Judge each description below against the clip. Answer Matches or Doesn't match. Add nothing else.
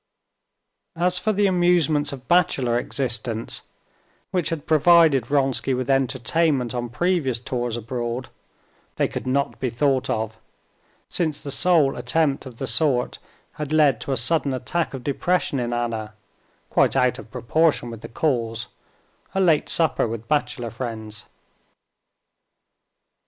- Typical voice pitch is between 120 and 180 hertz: Matches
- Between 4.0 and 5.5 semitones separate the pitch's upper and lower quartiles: Matches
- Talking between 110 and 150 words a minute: Matches